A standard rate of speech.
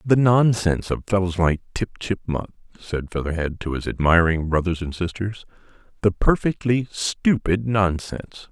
No: slow, 125 wpm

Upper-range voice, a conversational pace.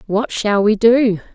Yes: high, 215 Hz; average, 180 wpm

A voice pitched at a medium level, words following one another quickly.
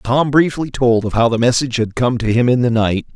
No: low, 120 Hz; fast, 265 wpm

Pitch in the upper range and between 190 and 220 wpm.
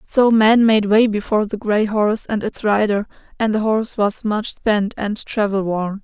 Yes: high, 210 Hz; average, 200 wpm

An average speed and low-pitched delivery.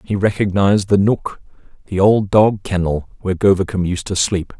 Yes: average, 170 wpm; very low, 95 Hz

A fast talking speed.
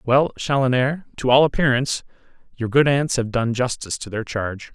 No: average, 175 wpm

